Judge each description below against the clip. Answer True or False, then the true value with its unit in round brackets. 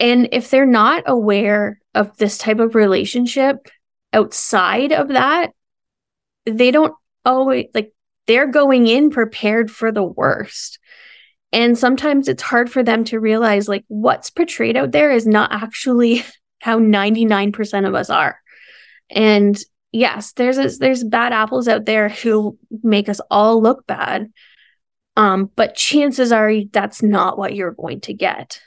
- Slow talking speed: False (155 wpm)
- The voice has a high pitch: True (225 Hz)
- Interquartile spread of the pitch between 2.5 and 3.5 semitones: True (3.2 semitones)